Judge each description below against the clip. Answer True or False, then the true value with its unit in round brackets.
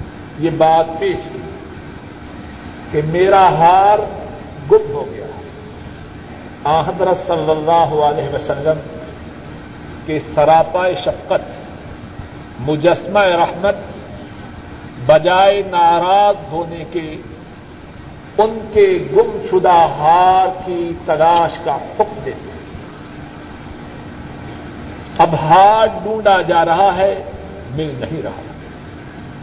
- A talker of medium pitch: True (175 Hz)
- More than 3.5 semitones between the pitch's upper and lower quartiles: True (4.3 semitones)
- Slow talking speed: True (90 wpm)